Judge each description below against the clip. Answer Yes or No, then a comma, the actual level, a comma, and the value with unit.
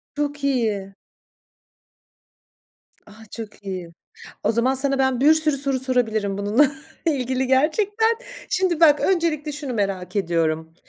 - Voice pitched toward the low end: No, very high, 260 Hz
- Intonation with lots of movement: Yes, wide, 6.4 semitones